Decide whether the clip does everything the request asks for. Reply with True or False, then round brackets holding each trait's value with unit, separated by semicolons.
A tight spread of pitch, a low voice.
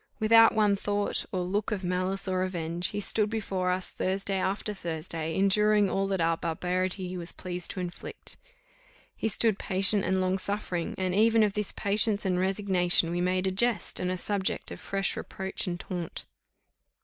False (2.1 semitones; 190 Hz)